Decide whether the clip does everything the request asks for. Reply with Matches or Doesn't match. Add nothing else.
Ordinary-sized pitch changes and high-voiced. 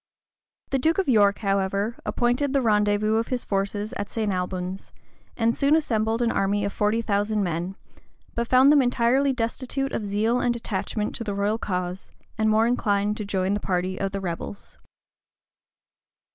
Matches